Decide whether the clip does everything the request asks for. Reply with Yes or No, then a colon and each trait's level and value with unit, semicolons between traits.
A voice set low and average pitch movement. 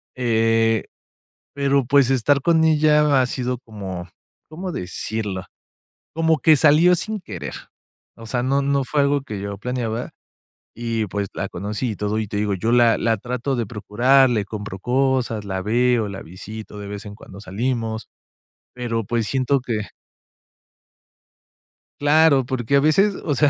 Yes: low, 120 Hz; average, 4.7 semitones